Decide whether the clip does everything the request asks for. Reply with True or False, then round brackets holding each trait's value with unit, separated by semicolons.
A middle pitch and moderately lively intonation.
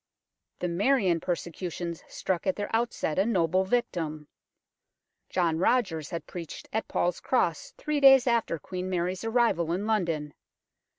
True (180 Hz; 5.0 semitones)